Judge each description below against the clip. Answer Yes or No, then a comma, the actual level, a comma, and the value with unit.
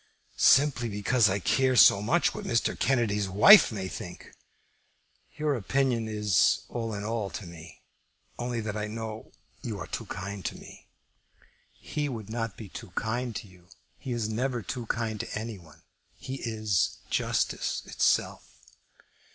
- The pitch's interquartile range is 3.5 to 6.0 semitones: No, average, 3.1 semitones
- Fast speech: No, average, 155 wpm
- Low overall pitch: Yes, low, 110 Hz